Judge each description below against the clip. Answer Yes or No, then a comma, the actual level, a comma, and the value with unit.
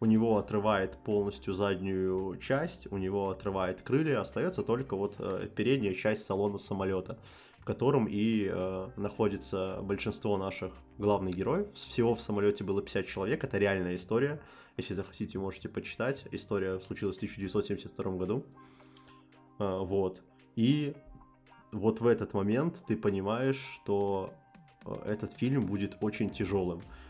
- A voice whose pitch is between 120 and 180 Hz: No, low, 100 Hz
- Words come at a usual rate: Yes, average, 125 wpm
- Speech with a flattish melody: Yes, narrow, 2.3 semitones